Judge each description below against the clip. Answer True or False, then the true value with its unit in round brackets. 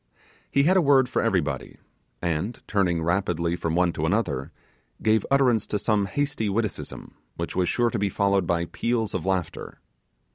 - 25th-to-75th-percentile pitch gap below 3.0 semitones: False (5.1 semitones)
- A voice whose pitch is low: True (100 Hz)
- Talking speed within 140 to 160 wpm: False (170 wpm)